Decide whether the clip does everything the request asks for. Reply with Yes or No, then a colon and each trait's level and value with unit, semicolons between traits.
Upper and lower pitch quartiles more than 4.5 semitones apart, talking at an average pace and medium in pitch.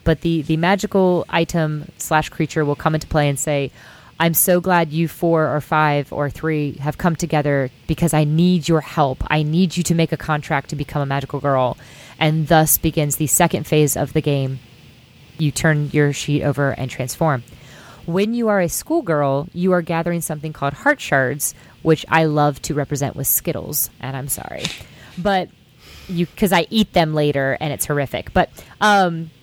No: average, 2.8 semitones; average, 190 wpm; medium, 155 Hz